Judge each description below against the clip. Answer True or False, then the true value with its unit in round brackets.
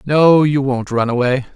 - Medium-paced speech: True (195 wpm)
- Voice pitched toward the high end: False (135 Hz)